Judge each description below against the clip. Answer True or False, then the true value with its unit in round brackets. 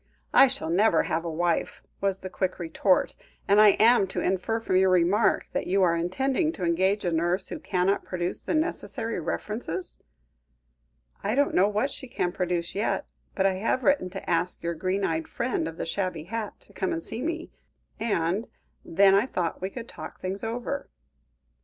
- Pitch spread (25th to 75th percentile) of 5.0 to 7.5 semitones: False (4.2 semitones)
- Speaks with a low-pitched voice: False (190 Hz)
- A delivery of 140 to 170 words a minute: False (190 wpm)